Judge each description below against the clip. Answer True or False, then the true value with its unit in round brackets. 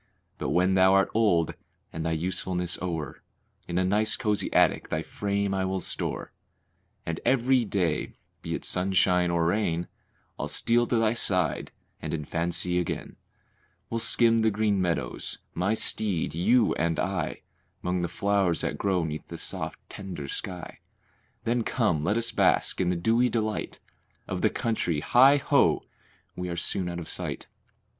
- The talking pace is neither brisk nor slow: True (165 wpm)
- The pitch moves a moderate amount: True (4.1 semitones)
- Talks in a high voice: False (95 Hz)